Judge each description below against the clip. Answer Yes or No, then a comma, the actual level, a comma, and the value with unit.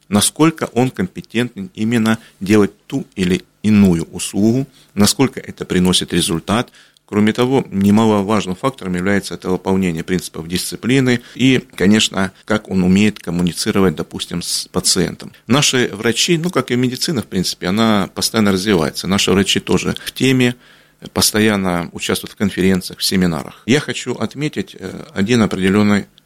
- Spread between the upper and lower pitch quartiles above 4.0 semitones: Yes, average, 4.7 semitones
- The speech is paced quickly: No, average, 135 wpm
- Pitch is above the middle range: No, low, 105 Hz